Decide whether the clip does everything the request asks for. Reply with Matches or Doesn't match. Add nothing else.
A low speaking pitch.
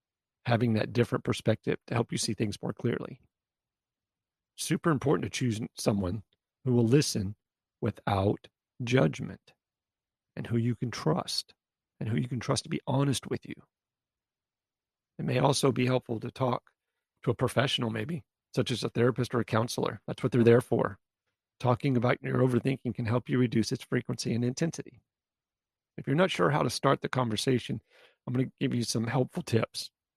Matches